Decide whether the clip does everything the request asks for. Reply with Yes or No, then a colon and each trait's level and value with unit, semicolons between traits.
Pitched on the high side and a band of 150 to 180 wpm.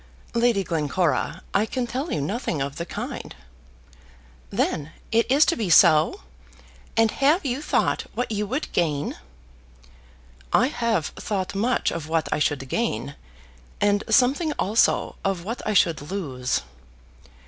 No: high, 205 Hz; average, 140 wpm